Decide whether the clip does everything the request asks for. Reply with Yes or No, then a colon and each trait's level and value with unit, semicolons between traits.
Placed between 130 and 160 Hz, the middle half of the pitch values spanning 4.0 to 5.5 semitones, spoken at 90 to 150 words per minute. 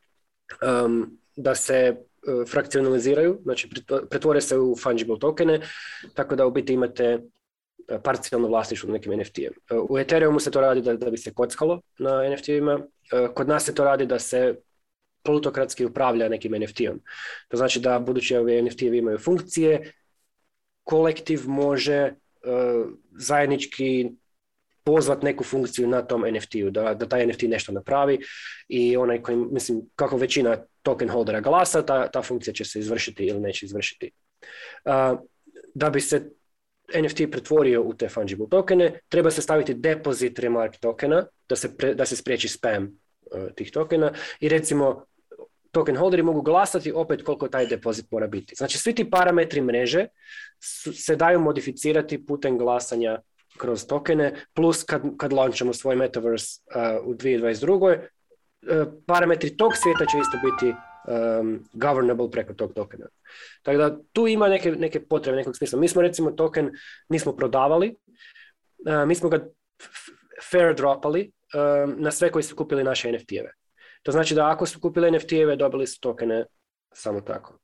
No: medium, 140 Hz; average, 4.7 semitones; fast, 160 wpm